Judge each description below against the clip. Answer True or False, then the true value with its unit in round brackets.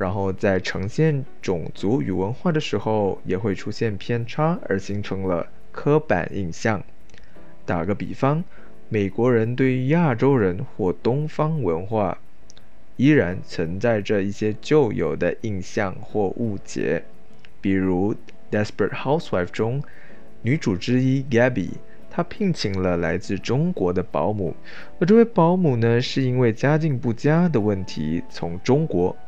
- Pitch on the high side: False (115 Hz)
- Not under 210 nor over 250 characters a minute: True (245 characters per minute)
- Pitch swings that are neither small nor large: False (6.8 semitones)